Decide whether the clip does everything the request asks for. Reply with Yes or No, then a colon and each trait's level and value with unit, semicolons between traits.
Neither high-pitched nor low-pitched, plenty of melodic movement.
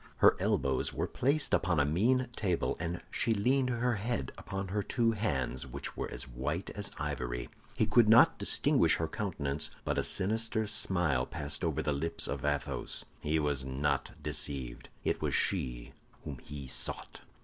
No: very low, 80 Hz; wide, 7.7 semitones